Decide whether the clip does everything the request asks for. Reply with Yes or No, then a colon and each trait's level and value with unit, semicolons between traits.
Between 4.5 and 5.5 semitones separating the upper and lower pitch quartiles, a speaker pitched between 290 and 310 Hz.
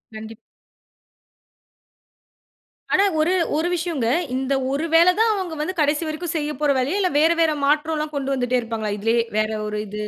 Yes: average, 4.9 semitones; very high, 300 Hz